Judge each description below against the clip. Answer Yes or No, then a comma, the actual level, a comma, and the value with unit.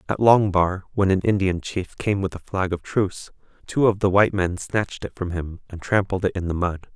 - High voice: No, very low, 95 Hz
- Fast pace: Yes, fast, 240 wpm